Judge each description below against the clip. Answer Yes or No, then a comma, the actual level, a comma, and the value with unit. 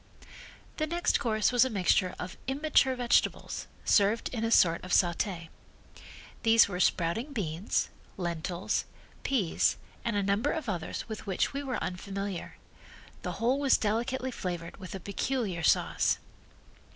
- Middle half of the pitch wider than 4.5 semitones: Yes, wide, 5.6 semitones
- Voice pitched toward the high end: Yes, high, 210 Hz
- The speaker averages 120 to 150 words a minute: Yes, average, 140 wpm